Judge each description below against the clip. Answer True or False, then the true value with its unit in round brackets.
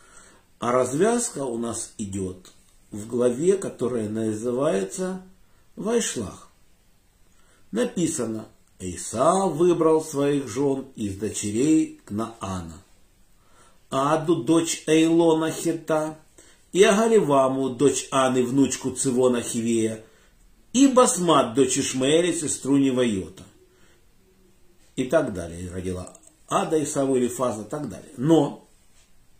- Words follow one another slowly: True (95 wpm)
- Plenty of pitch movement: True (7.2 semitones)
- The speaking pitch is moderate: False (130 Hz)